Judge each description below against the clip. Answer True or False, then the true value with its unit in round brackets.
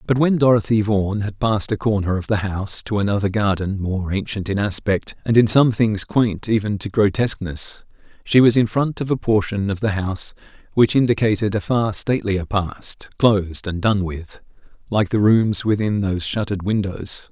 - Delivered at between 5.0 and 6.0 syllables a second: True (5.1 syllables/s)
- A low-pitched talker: True (105 Hz)